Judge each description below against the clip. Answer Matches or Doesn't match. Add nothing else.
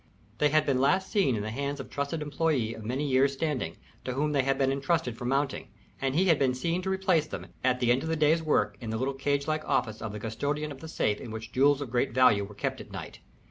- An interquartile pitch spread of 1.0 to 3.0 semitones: Doesn't match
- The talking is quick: Matches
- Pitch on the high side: Doesn't match